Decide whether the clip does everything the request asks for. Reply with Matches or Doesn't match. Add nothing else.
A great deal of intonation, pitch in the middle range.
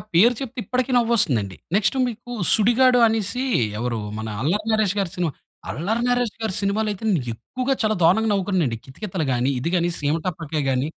Doesn't match